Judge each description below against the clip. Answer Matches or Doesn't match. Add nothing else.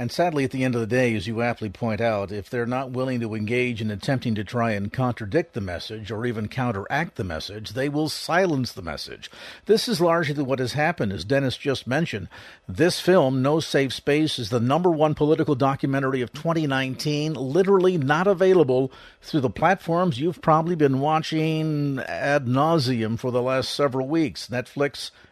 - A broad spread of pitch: Doesn't match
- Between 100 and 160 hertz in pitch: Matches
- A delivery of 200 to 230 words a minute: Doesn't match